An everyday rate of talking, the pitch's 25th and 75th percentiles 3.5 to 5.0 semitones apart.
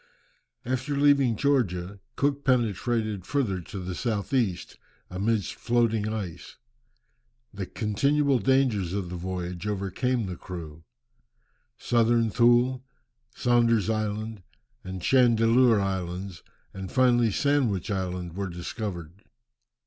No: slow, 105 wpm; average, 4.7 semitones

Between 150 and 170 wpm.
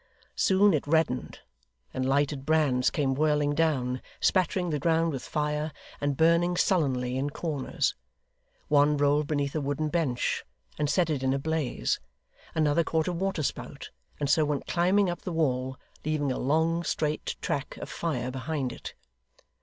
Yes: average, 160 wpm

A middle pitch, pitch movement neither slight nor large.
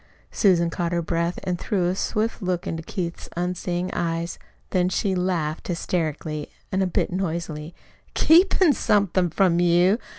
No: medium, 175 Hz; narrow, 1.9 semitones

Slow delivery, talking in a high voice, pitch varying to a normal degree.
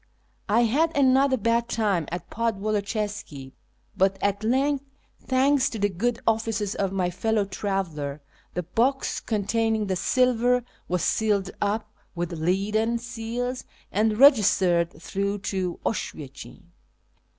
Yes: slow, 125 wpm; high, 215 Hz; average, 3.7 semitones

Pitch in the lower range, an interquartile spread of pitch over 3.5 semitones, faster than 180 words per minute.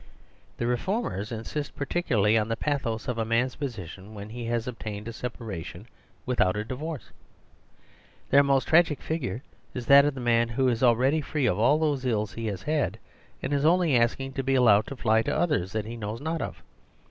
Yes: low, 120 Hz; average, 4.2 semitones; average, 195 wpm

